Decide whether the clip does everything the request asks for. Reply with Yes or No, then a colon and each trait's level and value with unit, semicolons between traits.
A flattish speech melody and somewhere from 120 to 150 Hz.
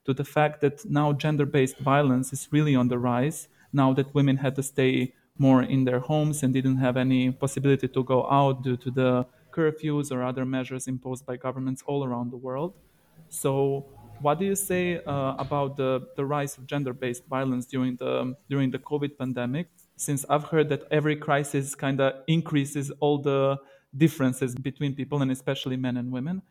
Yes: narrow, 2.1 semitones; low, 135 Hz